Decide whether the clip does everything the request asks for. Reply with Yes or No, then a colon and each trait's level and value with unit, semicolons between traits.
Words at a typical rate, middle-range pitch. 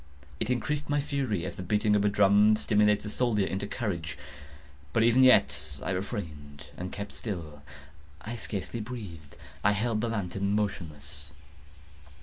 No: average, 150 wpm; low, 105 Hz